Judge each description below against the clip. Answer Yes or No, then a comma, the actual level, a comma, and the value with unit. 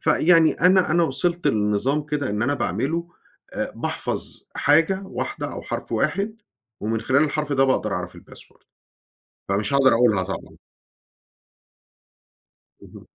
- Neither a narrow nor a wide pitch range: No, wide, 6.9 semitones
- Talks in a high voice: No, medium, 140 Hz